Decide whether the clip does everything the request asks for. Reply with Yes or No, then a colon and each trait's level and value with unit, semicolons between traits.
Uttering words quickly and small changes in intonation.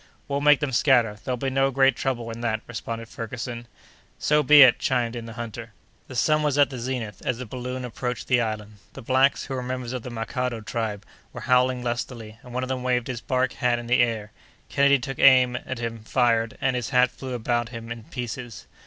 Yes: fast, 220 wpm; narrow, 1.9 semitones